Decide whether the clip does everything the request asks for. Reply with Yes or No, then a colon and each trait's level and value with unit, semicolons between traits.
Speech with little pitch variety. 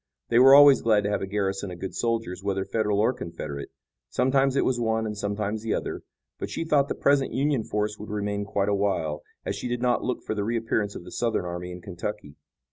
No: average, 3.5 semitones